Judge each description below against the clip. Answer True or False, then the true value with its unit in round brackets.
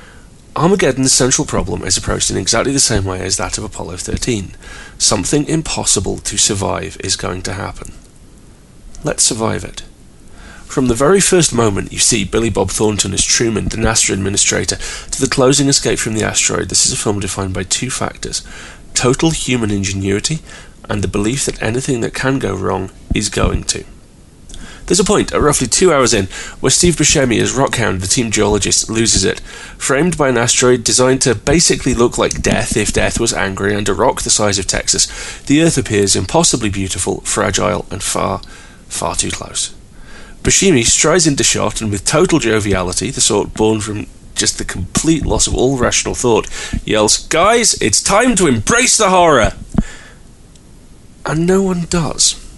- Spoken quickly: False (175 wpm)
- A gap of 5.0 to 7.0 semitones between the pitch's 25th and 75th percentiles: True (5.3 semitones)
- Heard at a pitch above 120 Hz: False (110 Hz)